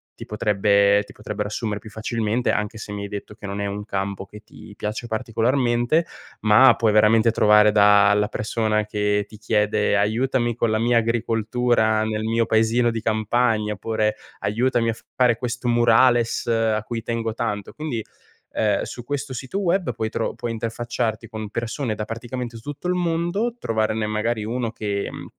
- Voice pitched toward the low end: Yes, low, 110 Hz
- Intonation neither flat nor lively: No, narrow, 2.0 semitones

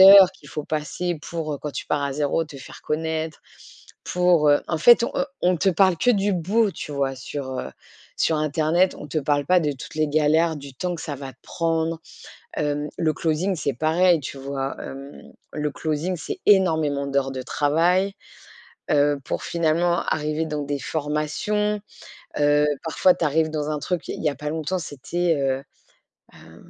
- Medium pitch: Yes, medium, 155 Hz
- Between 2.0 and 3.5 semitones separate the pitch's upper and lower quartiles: Yes, average, 3.1 semitones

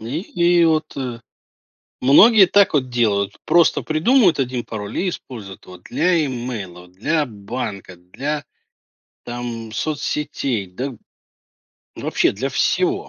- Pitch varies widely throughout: Yes, wide, 6.6 semitones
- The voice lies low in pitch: Yes, low, 125 Hz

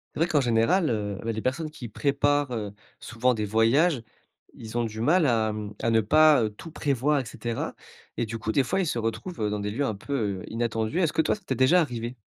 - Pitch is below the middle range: Yes, low, 120 Hz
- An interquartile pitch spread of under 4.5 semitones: No, average, 4.8 semitones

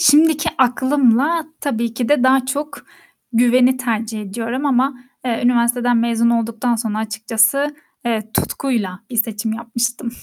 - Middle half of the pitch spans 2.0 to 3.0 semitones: Yes, narrow, 2.6 semitones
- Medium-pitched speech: No, high, 240 Hz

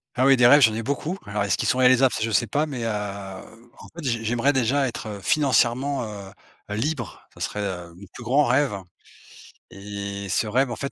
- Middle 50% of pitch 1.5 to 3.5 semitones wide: No, average, 4.6 semitones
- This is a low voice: Yes, low, 120 Hz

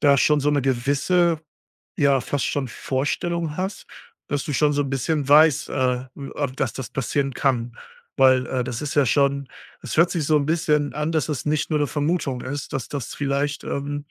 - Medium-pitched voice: Yes, medium, 145 Hz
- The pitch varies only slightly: Yes, narrow, 2.1 semitones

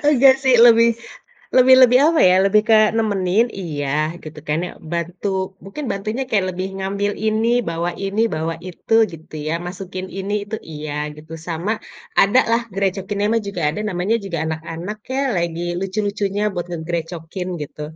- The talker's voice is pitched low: No, high, 195 Hz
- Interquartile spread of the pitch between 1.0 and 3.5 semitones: No, average, 4.2 semitones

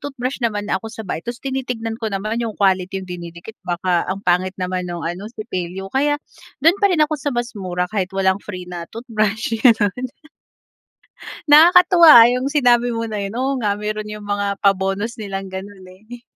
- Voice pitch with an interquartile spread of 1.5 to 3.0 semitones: No, average, 4.2 semitones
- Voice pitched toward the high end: Yes, high, 210 Hz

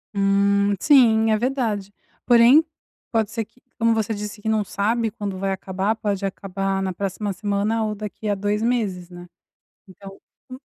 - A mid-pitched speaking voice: No, high, 205 Hz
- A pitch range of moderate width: No, narrow, 2.2 semitones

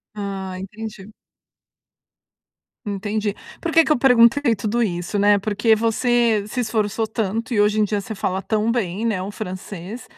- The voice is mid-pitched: No, high, 215 Hz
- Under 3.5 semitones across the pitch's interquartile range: Yes, narrow, 2.4 semitones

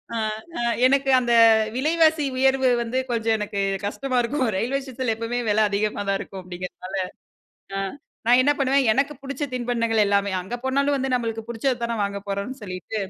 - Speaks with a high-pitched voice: Yes, high, 240 Hz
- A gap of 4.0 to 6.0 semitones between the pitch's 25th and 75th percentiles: Yes, average, 4.4 semitones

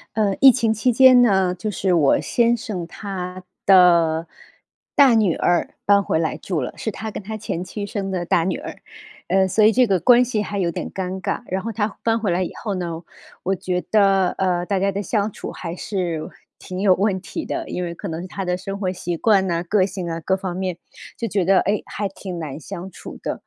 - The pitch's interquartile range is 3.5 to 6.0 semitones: No, average, 3.0 semitones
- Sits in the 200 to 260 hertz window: No, high, 190 Hz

